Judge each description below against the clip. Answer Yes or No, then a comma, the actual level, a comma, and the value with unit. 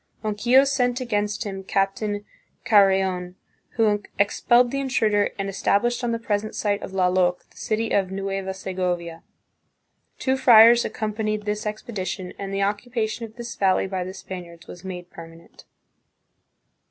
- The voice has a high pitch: Yes, high, 205 Hz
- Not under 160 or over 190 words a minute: No, average, 145 wpm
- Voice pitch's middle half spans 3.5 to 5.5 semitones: No, average, 3.0 semitones